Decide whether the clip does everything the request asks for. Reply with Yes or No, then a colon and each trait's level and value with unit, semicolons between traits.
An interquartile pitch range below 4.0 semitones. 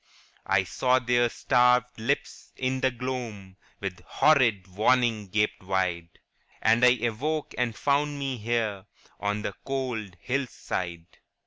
No: average, 4.4 semitones